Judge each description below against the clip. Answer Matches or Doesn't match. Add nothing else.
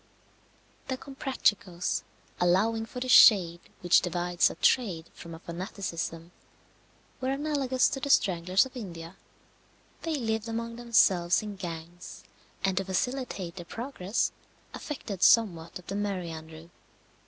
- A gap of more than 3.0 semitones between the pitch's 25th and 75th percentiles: Matches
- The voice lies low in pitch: Doesn't match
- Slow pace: Matches